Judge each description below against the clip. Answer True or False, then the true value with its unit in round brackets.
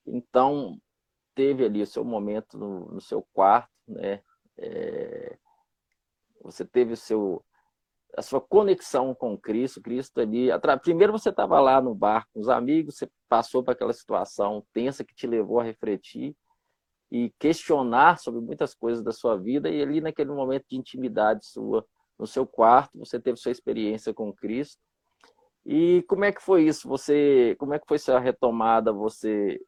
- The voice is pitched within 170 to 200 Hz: False (135 Hz)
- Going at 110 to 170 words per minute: True (165 wpm)